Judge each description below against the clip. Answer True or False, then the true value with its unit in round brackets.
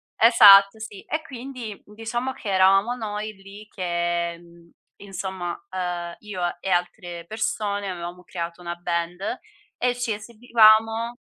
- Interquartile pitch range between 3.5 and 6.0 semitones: True (4.0 semitones)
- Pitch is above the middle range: True (195 Hz)